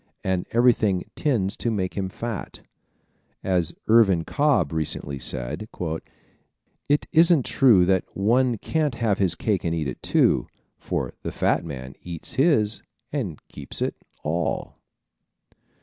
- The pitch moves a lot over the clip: Yes, wide, 5.9 semitones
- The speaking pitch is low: Yes, low, 100 Hz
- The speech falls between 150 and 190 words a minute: No, slow, 135 wpm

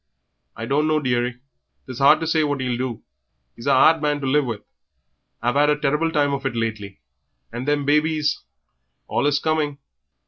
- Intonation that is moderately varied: Yes, average, 3.2 semitones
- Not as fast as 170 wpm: No, average, 175 wpm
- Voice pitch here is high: No, medium, 140 Hz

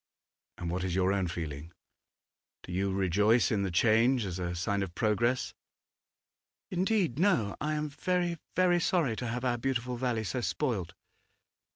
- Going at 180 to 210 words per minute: No, average, 160 wpm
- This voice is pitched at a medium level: No, low, 115 Hz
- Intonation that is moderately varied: No, wide, 6.1 semitones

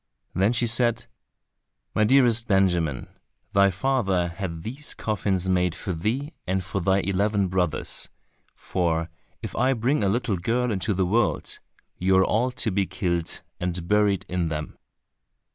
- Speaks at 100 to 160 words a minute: Yes, average, 155 wpm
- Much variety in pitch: No, average, 4.2 semitones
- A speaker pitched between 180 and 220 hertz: No, very low, 95 Hz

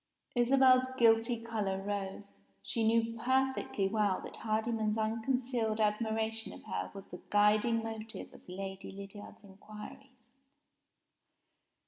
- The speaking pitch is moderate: No, high, 220 Hz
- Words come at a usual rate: No, slow, 110 wpm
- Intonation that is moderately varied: No, narrow, 2.1 semitones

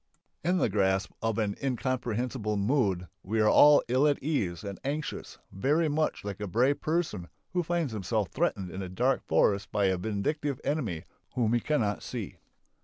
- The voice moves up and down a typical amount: No, wide, 6.4 semitones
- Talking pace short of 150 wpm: No, average, 170 wpm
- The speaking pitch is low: Yes, low, 115 Hz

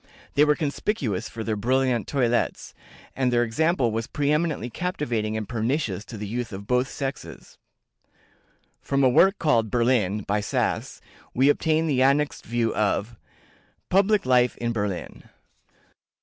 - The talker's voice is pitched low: Yes, low, 125 Hz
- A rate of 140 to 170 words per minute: Yes, average, 145 wpm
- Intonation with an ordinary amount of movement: Yes, average, 4.6 semitones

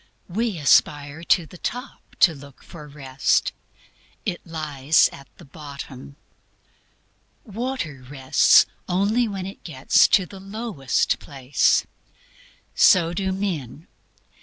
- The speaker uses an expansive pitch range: Yes, wide, 5.7 semitones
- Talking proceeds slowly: Yes, slow, 110 wpm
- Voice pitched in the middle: Yes, medium, 160 Hz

